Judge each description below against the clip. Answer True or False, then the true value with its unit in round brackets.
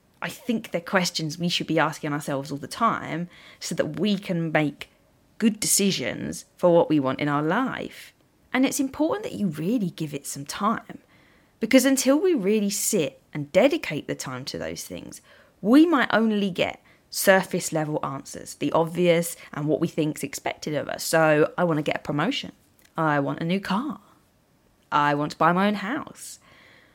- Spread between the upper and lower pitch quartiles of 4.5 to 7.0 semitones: True (5.1 semitones)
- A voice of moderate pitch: True (170 Hz)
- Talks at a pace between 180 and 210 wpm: True (185 wpm)